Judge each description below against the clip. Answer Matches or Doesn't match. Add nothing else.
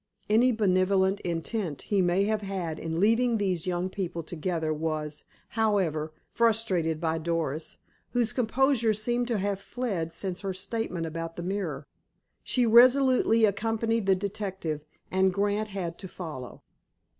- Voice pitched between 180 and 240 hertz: Matches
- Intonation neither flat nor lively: Matches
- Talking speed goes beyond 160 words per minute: Doesn't match